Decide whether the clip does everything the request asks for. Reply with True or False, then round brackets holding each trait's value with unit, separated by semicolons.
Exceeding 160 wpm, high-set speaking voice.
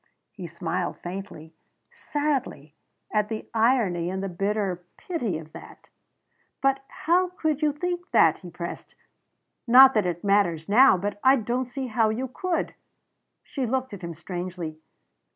False (150 wpm; 215 Hz)